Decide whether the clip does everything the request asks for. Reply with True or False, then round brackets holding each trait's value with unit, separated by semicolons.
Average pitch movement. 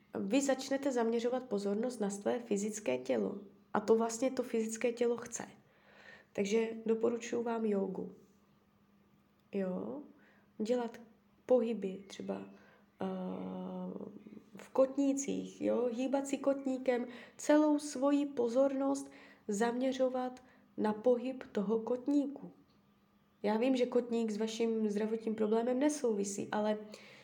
True (3.3 semitones)